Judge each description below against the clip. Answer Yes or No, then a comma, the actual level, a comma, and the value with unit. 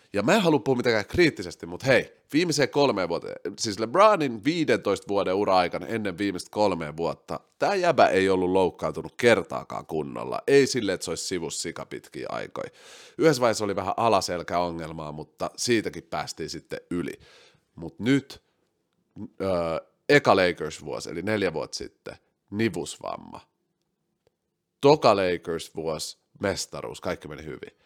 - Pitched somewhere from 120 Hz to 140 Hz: No, low, 105 Hz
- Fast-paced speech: No, average, 140 wpm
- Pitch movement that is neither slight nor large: No, wide, 7.8 semitones